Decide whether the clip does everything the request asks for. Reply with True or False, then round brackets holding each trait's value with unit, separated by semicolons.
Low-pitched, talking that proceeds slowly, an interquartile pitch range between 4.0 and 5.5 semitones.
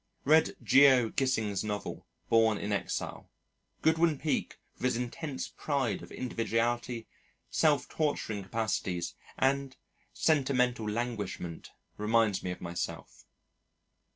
True (120 Hz; 105 wpm; 4.5 semitones)